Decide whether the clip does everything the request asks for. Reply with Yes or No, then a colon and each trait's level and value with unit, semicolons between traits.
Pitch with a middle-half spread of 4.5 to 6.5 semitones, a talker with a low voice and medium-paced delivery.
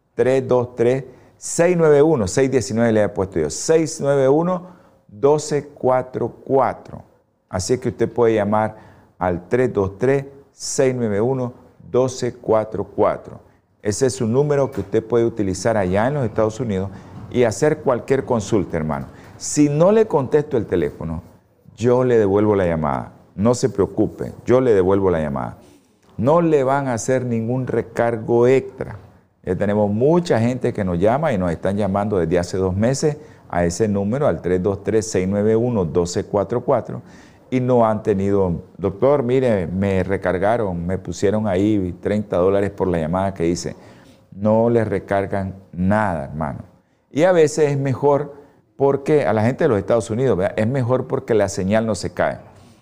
Yes: average, 4.9 semitones; low, 110 Hz; average, 140 wpm